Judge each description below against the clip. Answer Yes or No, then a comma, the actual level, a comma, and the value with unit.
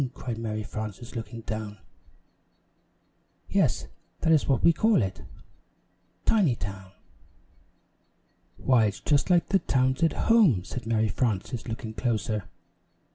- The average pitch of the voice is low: Yes, low, 115 Hz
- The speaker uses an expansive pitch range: No, average, 4.2 semitones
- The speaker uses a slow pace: Yes, slow, 120 wpm